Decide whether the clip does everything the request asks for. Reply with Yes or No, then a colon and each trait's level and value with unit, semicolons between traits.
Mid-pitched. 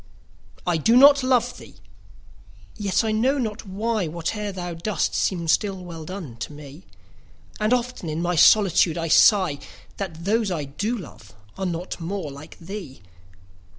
Yes: medium, 180 Hz